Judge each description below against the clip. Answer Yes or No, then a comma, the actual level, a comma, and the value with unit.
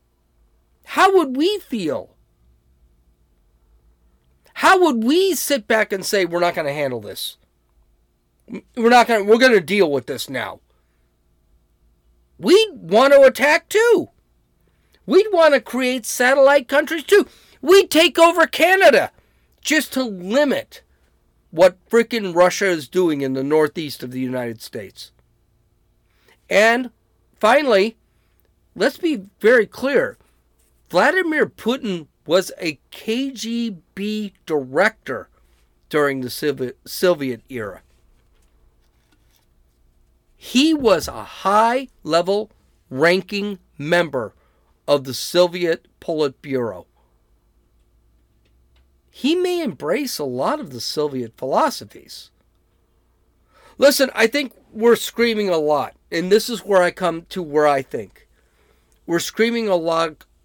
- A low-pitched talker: No, medium, 175 Hz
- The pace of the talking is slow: Yes, slow, 110 wpm